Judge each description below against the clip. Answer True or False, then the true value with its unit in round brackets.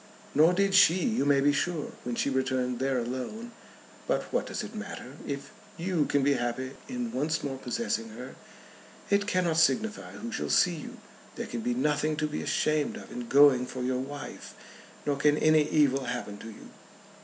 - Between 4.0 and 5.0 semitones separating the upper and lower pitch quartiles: True (4.6 semitones)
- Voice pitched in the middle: True (145 Hz)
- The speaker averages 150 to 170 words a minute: False (190 wpm)